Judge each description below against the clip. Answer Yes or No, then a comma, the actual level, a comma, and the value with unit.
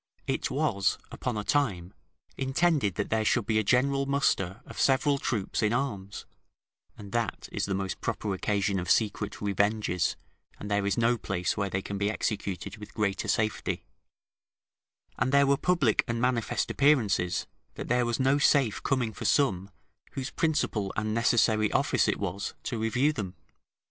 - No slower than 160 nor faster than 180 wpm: Yes, average, 165 wpm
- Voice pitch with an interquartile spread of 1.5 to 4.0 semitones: No, average, 4.7 semitones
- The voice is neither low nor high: No, low, 110 Hz